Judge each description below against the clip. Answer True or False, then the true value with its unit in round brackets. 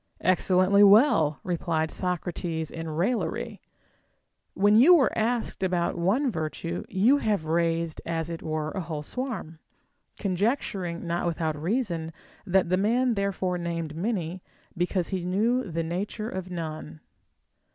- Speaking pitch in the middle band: True (180 Hz)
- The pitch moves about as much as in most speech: True (3.7 semitones)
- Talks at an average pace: False (130 wpm)